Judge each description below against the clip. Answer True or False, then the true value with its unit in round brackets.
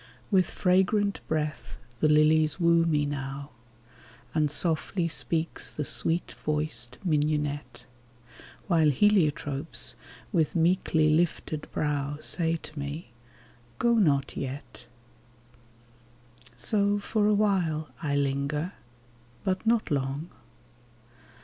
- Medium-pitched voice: True (155 Hz)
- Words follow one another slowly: True (100 wpm)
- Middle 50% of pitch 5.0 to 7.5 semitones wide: False (3.4 semitones)